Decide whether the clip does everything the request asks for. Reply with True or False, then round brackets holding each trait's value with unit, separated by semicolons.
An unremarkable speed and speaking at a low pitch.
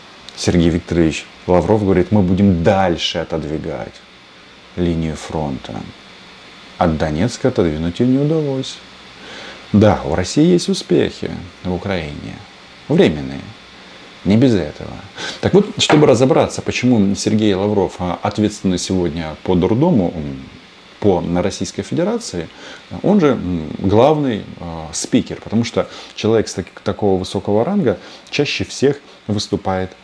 True (120 wpm; 95 Hz)